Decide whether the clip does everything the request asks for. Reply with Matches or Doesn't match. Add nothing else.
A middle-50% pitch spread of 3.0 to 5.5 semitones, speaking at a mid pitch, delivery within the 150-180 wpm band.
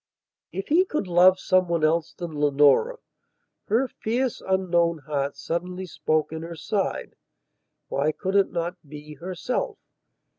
Doesn't match